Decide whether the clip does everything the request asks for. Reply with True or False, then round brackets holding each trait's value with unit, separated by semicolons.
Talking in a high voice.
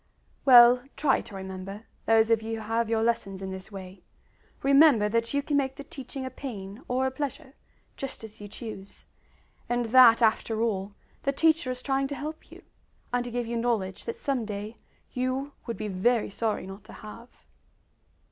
True (230 Hz)